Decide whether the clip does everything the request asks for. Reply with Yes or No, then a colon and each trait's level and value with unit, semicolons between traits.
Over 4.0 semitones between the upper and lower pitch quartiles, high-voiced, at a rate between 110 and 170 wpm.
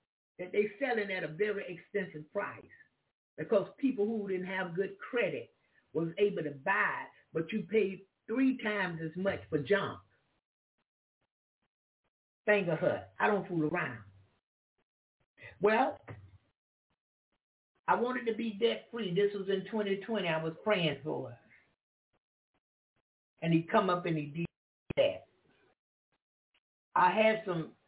Yes: average, 4.7 semitones; high, 195 Hz; slow, 135 wpm